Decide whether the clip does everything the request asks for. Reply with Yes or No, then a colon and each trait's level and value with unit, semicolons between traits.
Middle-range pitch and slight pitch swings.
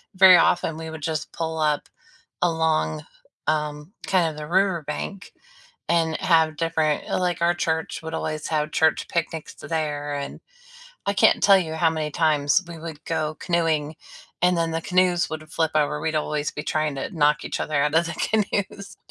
Yes: medium, 160 Hz; narrow, 2.0 semitones